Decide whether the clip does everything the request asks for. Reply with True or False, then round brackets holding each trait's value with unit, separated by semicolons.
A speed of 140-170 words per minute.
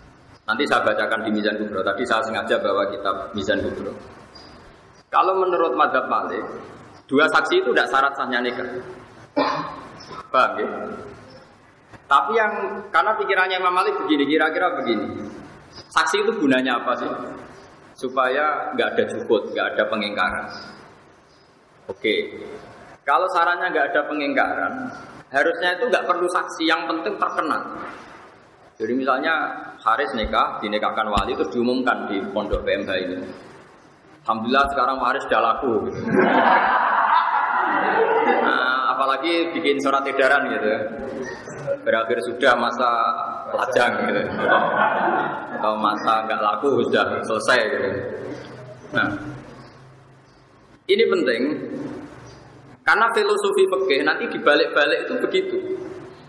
False (115 wpm)